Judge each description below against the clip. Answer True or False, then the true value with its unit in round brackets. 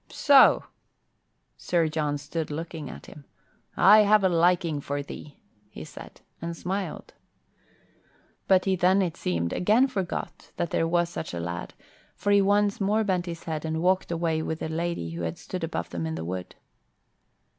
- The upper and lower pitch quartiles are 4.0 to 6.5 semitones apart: True (4.3 semitones)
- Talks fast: False (175 wpm)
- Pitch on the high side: False (170 Hz)